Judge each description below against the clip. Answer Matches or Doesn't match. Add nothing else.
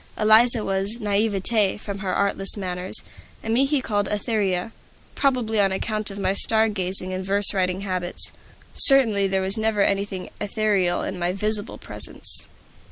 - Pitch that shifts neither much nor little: Doesn't match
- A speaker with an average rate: Matches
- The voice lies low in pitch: Doesn't match